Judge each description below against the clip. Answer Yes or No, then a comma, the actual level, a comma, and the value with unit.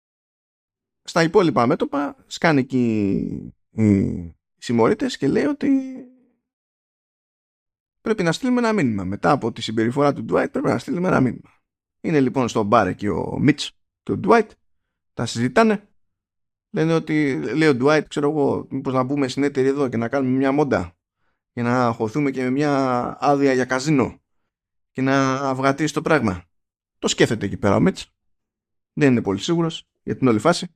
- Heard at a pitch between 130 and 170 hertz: Yes, low, 135 Hz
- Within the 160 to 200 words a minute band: Yes, average, 165 wpm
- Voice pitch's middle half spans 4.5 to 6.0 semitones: Yes, wide, 5.5 semitones